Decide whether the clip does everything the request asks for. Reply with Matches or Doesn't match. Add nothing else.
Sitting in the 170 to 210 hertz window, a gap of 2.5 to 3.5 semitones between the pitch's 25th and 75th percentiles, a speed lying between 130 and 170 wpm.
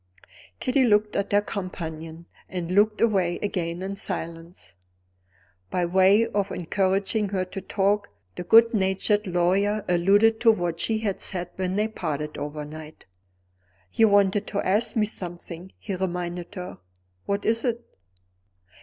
Matches